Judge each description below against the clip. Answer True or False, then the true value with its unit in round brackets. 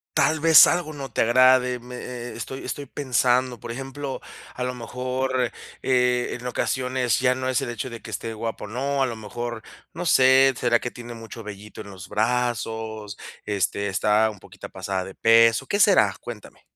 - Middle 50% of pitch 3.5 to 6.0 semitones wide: False (2.6 semitones)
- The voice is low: True (125 Hz)